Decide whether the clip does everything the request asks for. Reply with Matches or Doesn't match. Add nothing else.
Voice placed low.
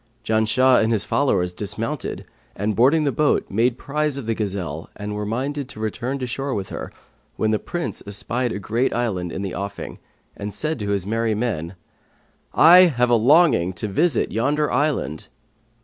Matches